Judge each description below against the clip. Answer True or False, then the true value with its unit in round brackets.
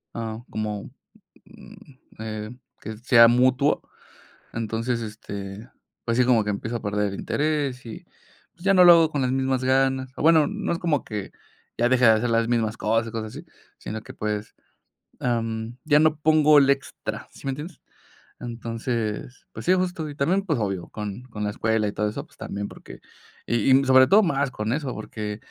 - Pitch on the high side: False (120 Hz)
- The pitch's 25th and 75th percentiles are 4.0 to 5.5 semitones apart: True (4.4 semitones)